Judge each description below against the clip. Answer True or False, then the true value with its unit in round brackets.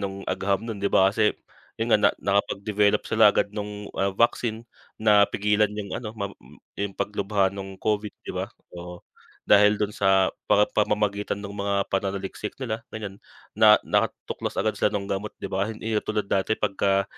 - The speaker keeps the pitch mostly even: True (1.4 semitones)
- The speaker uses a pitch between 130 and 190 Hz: False (100 Hz)